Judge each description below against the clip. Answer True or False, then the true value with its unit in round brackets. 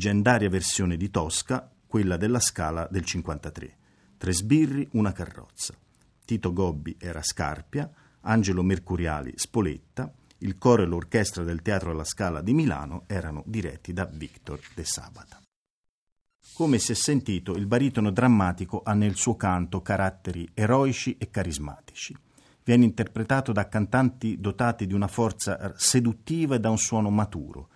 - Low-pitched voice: True (100 Hz)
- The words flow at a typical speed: True (140 wpm)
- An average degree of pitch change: True (4.8 semitones)